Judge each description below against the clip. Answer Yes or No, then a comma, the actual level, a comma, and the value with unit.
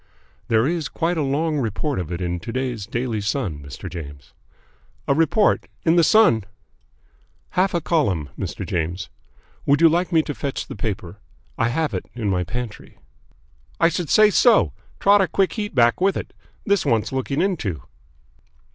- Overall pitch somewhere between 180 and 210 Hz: No, low, 135 Hz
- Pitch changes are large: Yes, wide, 8.8 semitones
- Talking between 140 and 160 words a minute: No, average, 175 wpm